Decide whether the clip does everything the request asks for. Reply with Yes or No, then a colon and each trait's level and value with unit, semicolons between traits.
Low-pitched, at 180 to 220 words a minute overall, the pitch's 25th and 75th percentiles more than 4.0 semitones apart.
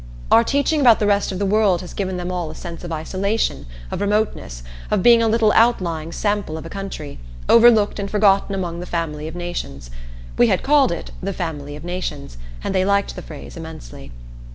No: medium, 185 Hz; average, 200 wpm; average, 4.5 semitones